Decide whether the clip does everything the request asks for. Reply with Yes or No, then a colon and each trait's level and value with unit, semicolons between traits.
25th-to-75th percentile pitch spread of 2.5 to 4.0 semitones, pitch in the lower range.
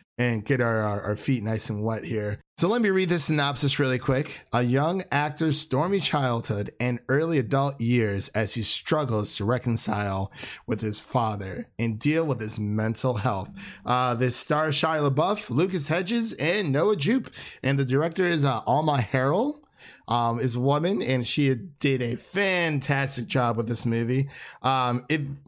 No: average, 4.5 semitones; low, 130 Hz